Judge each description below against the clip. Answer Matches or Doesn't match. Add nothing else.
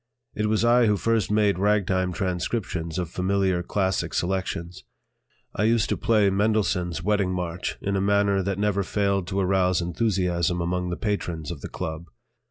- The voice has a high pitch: Doesn't match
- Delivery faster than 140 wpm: Matches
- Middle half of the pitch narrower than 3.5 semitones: Matches